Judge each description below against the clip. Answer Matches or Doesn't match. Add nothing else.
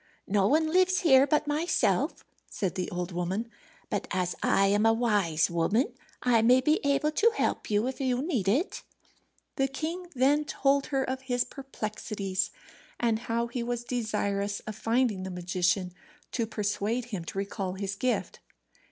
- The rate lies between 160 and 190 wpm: Matches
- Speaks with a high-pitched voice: Matches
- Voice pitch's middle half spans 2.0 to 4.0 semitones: Doesn't match